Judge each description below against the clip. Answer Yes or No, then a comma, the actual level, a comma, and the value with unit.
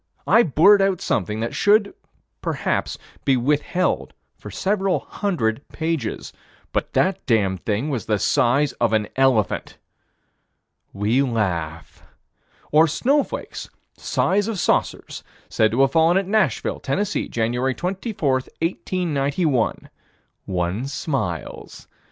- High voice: No, medium, 140 Hz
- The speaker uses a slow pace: Yes, slow, 115 wpm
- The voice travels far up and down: Yes, wide, 8.6 semitones